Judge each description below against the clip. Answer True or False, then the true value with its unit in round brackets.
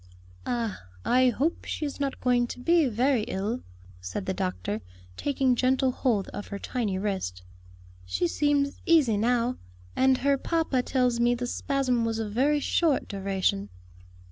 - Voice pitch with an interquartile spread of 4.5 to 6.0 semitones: True (4.9 semitones)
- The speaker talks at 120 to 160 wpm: True (155 wpm)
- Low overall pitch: False (245 Hz)